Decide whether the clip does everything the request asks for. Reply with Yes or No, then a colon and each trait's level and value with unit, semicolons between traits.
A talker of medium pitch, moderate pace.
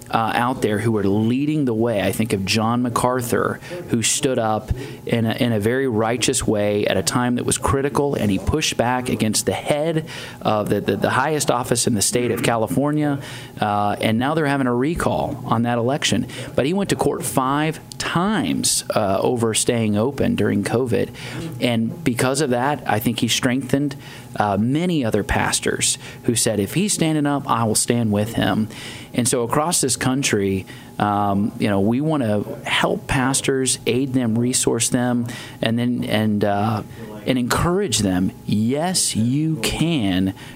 No: low, 125 Hz; average, 180 wpm